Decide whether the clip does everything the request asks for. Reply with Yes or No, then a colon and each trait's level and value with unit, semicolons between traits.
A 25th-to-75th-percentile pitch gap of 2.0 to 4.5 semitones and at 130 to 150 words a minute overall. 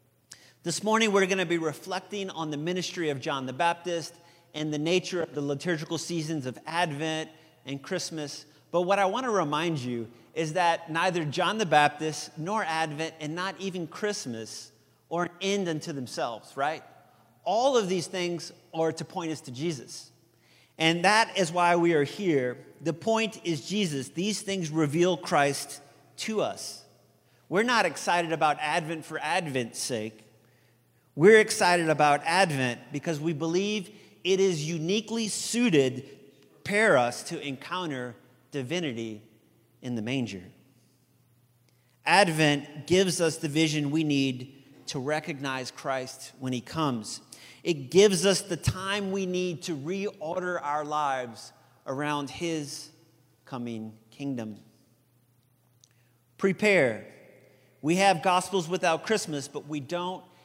No: average, 4.9 semitones; average, 140 wpm